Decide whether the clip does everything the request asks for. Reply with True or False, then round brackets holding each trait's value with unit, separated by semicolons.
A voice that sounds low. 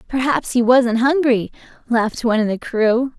False (240 Hz)